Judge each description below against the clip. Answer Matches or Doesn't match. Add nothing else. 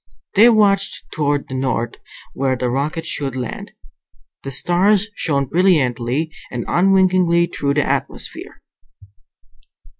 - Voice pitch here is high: Doesn't match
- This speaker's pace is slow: Matches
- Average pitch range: Doesn't match